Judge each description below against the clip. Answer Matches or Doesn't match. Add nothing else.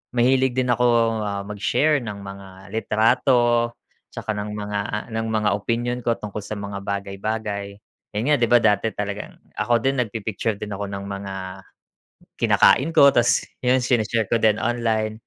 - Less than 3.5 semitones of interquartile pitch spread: Matches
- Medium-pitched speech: Doesn't match